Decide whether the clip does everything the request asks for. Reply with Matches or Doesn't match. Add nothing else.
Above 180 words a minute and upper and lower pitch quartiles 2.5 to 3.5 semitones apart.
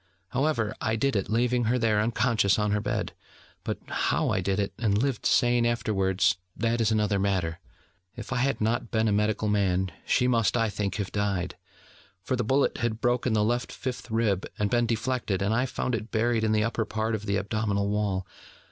Matches